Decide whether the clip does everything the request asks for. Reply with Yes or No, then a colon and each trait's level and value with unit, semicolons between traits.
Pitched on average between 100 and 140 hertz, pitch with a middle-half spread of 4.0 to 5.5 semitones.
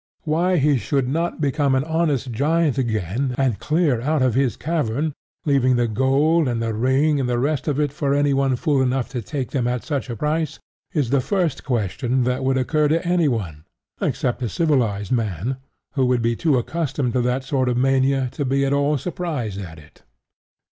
No: low, 135 Hz; average, 3.4 semitones